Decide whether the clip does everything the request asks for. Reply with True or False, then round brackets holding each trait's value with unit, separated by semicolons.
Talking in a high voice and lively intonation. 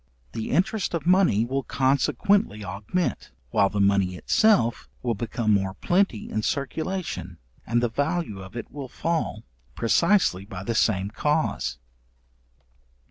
False (120 Hz; 8.6 semitones)